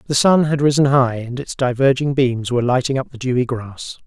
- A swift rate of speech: Yes, fast, 220 wpm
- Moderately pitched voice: No, low, 130 Hz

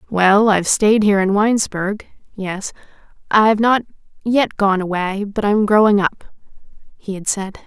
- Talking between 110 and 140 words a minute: Yes, slow, 135 wpm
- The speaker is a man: No, female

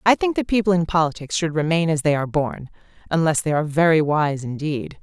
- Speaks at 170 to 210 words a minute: Yes, fast, 205 wpm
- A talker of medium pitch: Yes, medium, 160 Hz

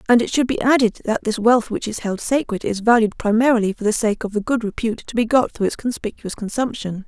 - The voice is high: Yes, high, 225 Hz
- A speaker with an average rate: No, fast, 245 wpm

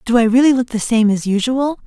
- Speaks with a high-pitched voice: Yes, high, 235 Hz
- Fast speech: Yes, fast, 260 wpm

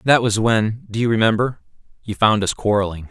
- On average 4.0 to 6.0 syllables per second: Yes, 5.5 syllables/s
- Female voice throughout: No, male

